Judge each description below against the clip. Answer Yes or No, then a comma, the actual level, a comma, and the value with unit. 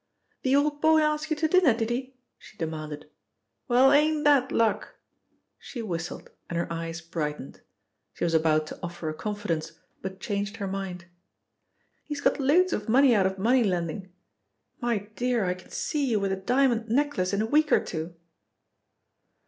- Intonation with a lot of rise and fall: Yes, wide, 7.6 semitones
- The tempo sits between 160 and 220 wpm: Yes, average, 175 wpm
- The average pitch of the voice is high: Yes, high, 215 Hz